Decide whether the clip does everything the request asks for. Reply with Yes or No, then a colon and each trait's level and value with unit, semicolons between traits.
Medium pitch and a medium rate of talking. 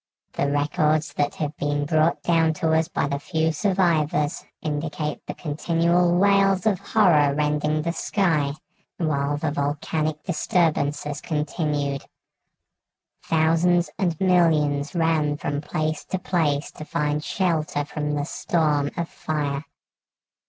No: medium, 155 Hz; slow, 125 wpm